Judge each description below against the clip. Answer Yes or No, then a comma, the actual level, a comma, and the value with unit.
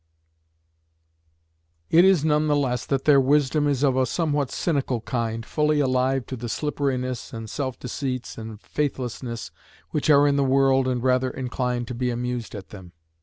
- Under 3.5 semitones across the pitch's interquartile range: Yes, average, 2.7 semitones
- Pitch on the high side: No, low, 130 Hz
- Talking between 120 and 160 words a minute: No, average, 170 wpm